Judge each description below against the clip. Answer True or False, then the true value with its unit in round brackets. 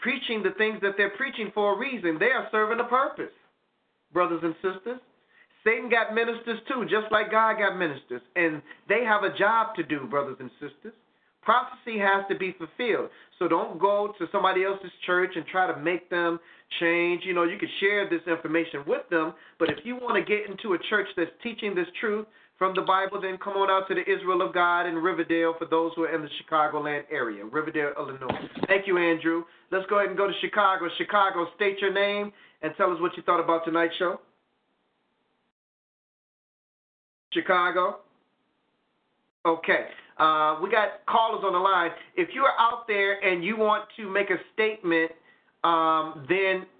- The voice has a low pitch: False (190 Hz)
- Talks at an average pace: True (185 wpm)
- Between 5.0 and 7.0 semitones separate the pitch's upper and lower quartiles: False (4.1 semitones)